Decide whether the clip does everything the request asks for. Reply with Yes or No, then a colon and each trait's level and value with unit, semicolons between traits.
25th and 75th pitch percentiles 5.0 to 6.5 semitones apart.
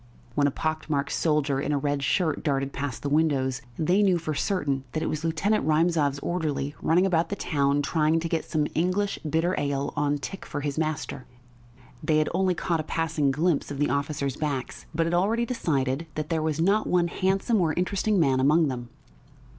No: average, 3.2 semitones